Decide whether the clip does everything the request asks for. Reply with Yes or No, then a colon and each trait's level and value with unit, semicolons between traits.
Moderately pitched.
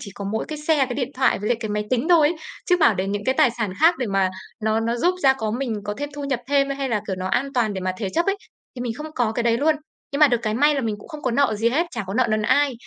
No: high, 245 Hz